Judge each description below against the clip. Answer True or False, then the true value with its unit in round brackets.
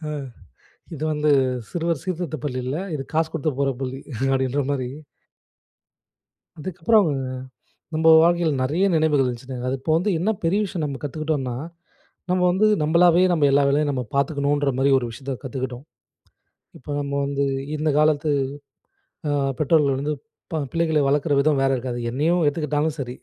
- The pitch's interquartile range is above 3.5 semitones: False (3.1 semitones)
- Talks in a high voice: False (145 Hz)